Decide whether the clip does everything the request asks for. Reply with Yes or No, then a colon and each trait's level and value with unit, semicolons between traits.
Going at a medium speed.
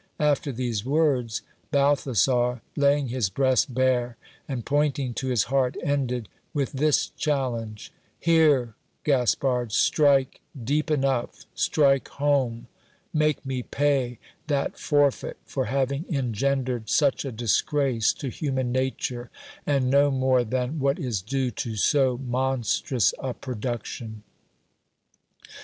No: slow, 120 wpm